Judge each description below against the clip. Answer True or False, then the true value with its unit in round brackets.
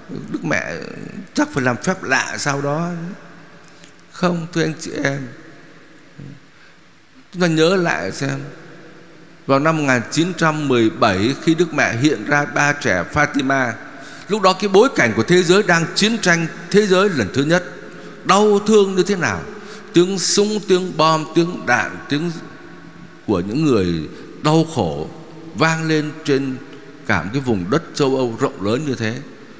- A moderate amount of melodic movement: True (4.2 semitones)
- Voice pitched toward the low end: False (160 Hz)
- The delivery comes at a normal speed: False (155 wpm)